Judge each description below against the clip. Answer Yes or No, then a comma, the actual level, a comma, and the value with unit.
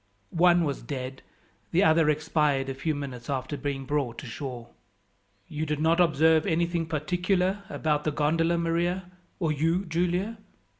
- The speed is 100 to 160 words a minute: Yes, average, 145 wpm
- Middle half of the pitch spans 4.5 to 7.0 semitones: No, average, 3.2 semitones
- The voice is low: No, medium, 155 Hz